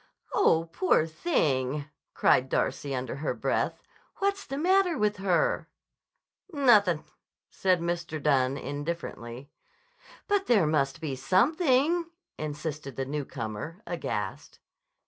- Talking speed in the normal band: No, slow, 105 wpm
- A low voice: No, medium, 160 Hz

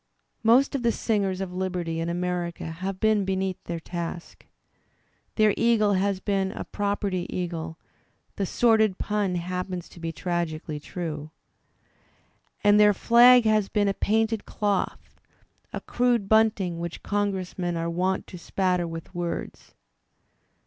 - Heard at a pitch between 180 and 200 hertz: Yes, high, 190 Hz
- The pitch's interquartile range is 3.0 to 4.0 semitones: Yes, average, 3.3 semitones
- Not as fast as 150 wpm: Yes, average, 140 wpm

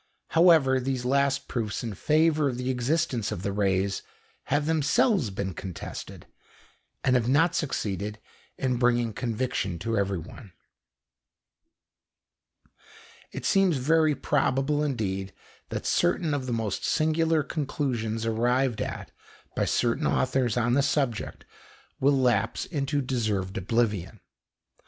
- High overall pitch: No, low, 125 Hz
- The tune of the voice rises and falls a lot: No, average, 4.9 semitones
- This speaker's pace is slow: Yes, slow, 120 wpm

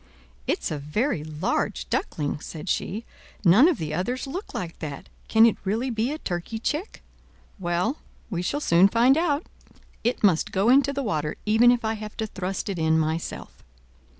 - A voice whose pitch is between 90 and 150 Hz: No, high, 210 Hz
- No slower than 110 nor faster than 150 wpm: No, average, 180 wpm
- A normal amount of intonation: No, wide, 7.0 semitones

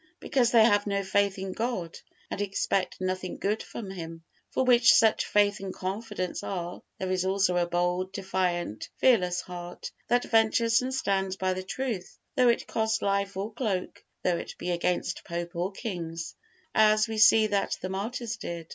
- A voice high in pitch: Yes, high, 195 Hz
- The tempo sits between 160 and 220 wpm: Yes, average, 175 wpm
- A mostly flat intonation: No, average, 3.4 semitones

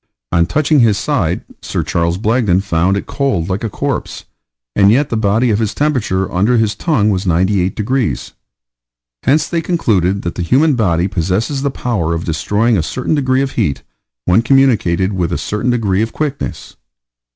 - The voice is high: No, low, 105 Hz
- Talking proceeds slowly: No, average, 175 wpm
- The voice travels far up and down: Yes, wide, 5.8 semitones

